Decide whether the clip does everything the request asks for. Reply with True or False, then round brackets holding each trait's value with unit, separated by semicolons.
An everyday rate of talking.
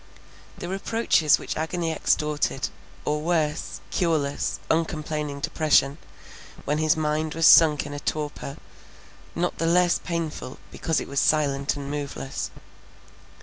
False (125 wpm)